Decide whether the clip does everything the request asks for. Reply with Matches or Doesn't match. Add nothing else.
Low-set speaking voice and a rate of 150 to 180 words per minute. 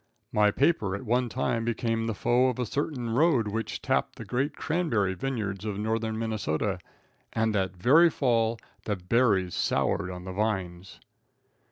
Matches